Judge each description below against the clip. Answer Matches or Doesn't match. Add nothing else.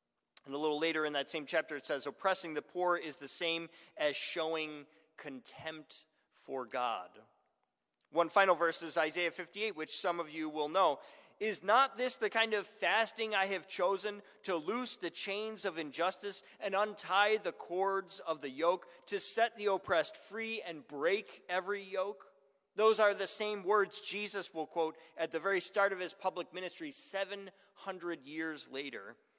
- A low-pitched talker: Doesn't match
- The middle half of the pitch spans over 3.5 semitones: Matches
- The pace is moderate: Matches